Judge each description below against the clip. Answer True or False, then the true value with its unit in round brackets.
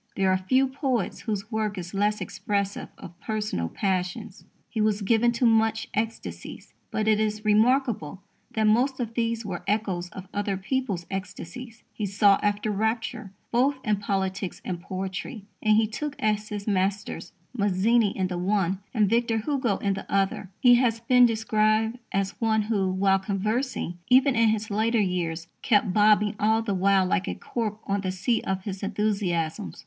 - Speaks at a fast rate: False (170 wpm)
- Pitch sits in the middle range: False (210 Hz)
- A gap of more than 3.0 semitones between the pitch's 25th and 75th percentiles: False (2.7 semitones)